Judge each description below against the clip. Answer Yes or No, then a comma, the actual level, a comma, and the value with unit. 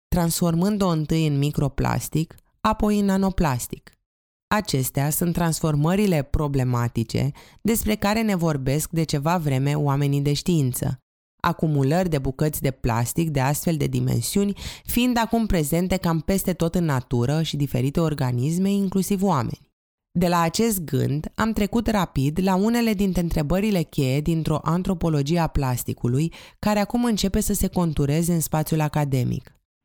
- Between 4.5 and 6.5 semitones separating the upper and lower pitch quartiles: Yes, average, 5.1 semitones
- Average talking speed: Yes, average, 135 wpm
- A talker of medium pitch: Yes, medium, 160 Hz